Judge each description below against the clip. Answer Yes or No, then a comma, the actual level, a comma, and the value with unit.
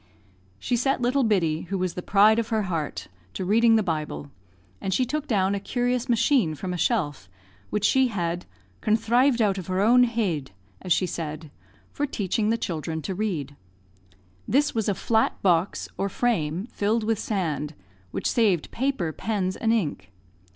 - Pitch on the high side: Yes, high, 200 Hz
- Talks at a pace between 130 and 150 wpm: No, average, 170 wpm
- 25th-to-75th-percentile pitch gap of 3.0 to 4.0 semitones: No, average, 5.2 semitones